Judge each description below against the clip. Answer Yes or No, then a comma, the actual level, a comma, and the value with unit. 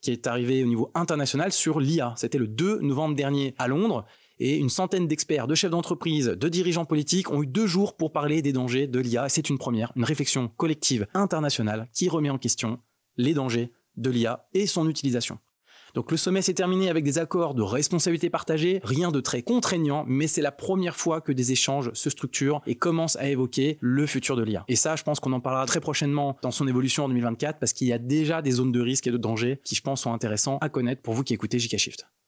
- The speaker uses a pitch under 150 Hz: Yes, medium, 140 Hz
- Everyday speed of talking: No, fast, 230 wpm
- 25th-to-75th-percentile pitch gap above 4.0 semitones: Yes, average, 4.4 semitones